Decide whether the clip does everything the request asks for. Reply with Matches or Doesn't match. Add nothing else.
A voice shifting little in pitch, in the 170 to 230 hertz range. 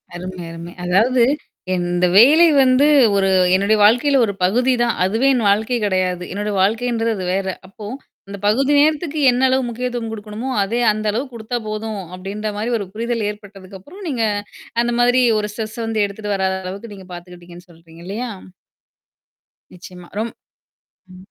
Doesn't match